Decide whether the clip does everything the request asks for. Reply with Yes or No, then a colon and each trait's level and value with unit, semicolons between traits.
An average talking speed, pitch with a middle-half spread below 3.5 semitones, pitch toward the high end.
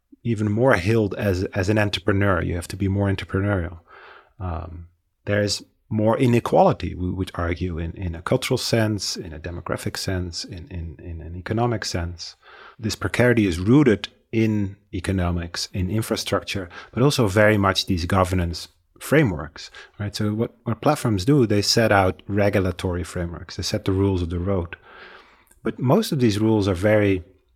No: average, 165 wpm; average, 3.1 semitones; low, 100 Hz